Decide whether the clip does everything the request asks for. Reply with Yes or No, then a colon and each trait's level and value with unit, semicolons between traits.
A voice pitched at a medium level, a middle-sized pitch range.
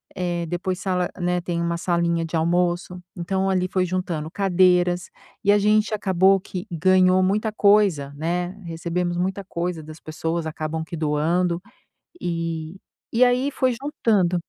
No: medium, 180 Hz; narrow, 2.0 semitones